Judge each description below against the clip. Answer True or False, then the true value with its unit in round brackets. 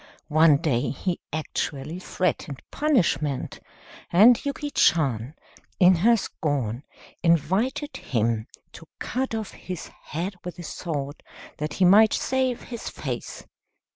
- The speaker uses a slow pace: True (120 wpm)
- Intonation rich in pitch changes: True (7.0 semitones)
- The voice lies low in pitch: False (170 Hz)